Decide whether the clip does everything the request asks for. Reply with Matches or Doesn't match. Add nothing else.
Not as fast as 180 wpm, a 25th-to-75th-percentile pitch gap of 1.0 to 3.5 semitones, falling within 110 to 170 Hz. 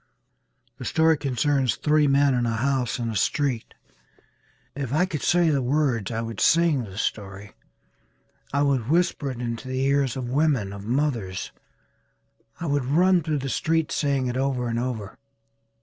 Doesn't match